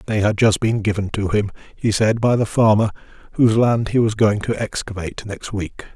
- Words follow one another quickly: Yes, fast, 210 wpm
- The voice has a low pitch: Yes, low, 105 Hz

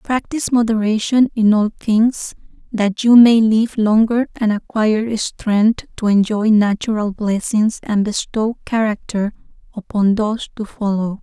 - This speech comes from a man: No, female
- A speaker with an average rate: No, slow, 130 wpm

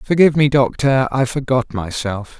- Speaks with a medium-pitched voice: No, low, 130 Hz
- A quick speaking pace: No, average, 150 wpm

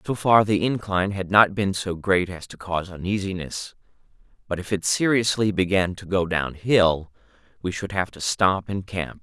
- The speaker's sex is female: No, male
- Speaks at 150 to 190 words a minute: Yes, average, 180 wpm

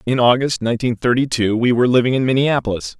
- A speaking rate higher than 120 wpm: Yes, average, 200 wpm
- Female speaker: No, male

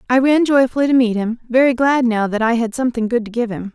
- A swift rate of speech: Yes, fast, 275 wpm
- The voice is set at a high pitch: Yes, high, 240 Hz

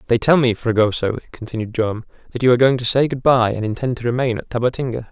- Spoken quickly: Yes, fast, 235 wpm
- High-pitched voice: No, low, 120 Hz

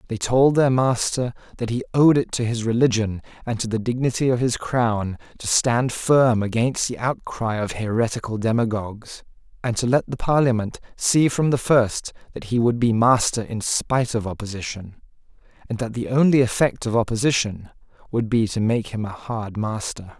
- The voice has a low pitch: Yes, low, 115 Hz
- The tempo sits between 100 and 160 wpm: No, average, 180 wpm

